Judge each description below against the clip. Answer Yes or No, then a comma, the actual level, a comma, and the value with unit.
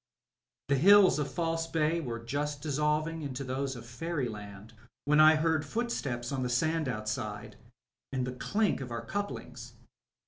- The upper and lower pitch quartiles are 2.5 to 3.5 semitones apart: No, average, 4.8 semitones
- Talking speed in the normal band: Yes, average, 150 wpm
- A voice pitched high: No, medium, 140 Hz